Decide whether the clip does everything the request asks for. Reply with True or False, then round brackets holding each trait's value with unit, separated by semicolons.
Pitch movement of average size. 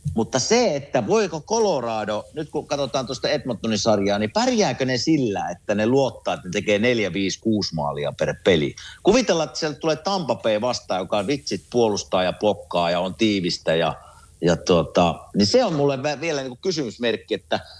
False (6.1 semitones)